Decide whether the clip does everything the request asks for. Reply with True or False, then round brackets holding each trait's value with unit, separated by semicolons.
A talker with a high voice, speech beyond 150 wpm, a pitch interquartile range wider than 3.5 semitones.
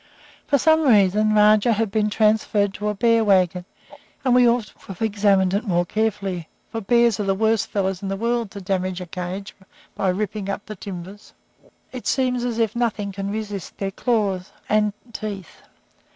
False (210 Hz; 180 wpm; 2.5 semitones)